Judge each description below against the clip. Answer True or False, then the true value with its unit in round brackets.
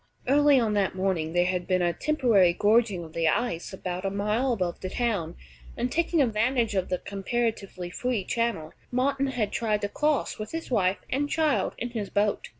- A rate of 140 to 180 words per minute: False (190 wpm)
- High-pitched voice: True (210 Hz)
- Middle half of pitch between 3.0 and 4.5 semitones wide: False (5.0 semitones)